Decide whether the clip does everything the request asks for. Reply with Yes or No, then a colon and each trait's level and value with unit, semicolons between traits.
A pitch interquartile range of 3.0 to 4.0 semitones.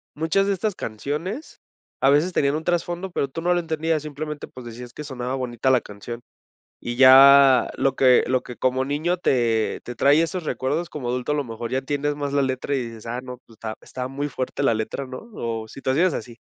Yes: average, 3.7 semitones